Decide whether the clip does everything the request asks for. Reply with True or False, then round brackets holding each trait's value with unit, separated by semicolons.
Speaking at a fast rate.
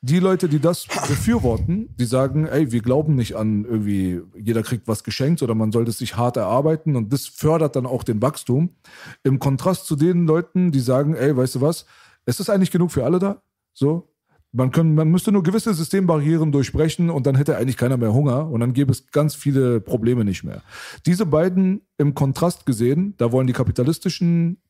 True (205 wpm)